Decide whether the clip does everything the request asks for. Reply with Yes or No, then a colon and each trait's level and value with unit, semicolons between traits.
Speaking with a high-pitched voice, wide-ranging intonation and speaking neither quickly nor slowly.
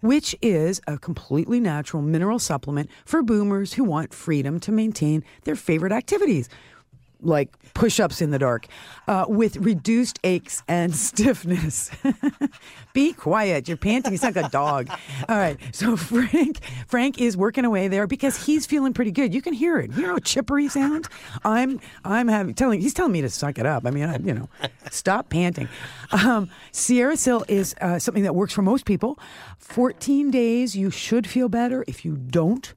Yes: high, 210 Hz; wide, 7.1 semitones; average, 180 wpm